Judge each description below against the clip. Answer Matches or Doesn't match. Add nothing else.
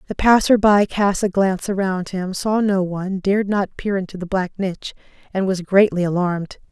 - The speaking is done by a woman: Matches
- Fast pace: Doesn't match